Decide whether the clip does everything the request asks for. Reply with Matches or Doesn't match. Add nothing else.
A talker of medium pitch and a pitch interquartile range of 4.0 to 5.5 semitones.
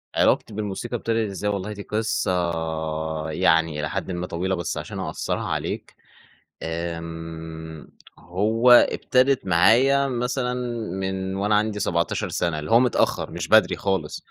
Doesn't match